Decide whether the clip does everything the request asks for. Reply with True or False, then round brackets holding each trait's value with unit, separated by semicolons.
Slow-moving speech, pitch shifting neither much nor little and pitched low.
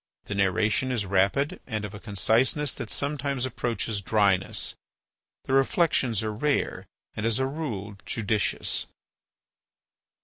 True (125 wpm; 4.7 semitones; 110 Hz)